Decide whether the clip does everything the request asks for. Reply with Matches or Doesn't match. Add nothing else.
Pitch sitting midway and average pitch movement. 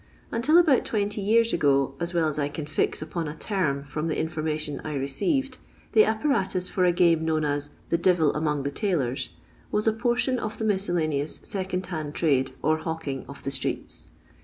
Doesn't match